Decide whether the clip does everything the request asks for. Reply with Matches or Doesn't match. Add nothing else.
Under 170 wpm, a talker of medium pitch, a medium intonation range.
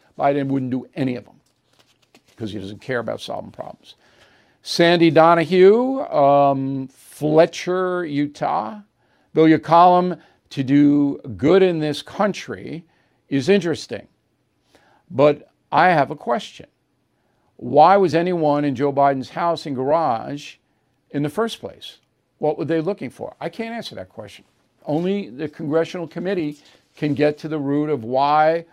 Matches